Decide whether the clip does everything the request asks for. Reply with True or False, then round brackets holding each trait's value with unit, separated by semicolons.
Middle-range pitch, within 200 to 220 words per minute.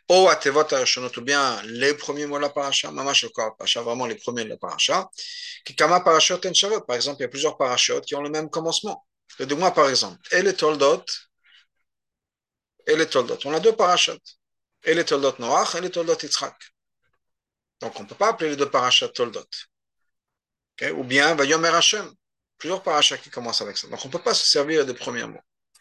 True (165 Hz; 215 wpm)